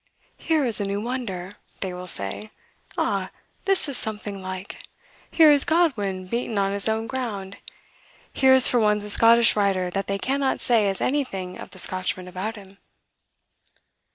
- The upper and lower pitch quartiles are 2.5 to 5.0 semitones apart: Yes, average, 4.6 semitones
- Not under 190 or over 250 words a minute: No, average, 165 wpm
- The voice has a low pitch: No, high, 210 Hz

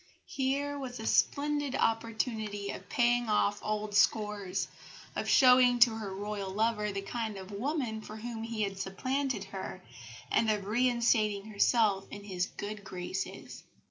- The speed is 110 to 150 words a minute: Yes, average, 145 wpm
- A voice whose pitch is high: Yes, high, 220 Hz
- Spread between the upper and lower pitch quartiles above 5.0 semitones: No, average, 3.1 semitones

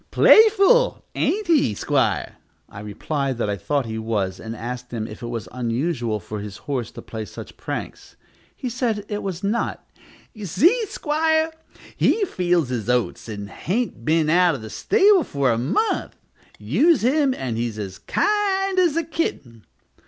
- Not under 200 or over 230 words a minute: No, average, 165 wpm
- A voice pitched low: No, medium, 150 Hz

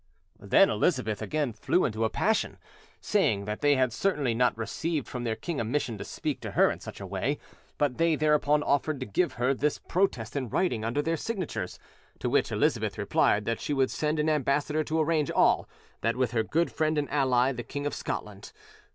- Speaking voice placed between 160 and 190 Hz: No, medium, 140 Hz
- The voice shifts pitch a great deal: No, average, 4.9 semitones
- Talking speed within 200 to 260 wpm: Yes, fast, 205 wpm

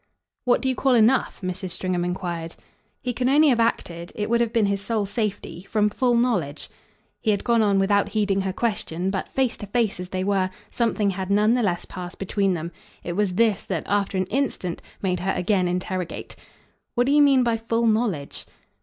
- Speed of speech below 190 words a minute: No, fast, 205 wpm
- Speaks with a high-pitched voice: Yes, high, 200 Hz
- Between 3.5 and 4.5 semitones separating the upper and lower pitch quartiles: Yes, average, 4.0 semitones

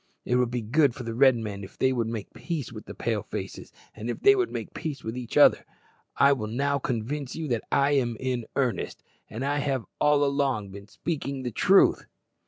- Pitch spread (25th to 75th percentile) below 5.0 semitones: Yes, average, 3.6 semitones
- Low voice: Yes, low, 130 Hz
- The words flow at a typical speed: No, fast, 210 wpm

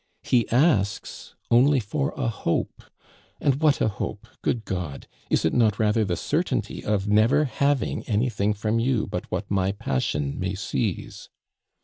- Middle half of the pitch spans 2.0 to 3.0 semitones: No, average, 4.3 semitones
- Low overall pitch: Yes, low, 105 Hz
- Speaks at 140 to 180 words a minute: Yes, average, 150 wpm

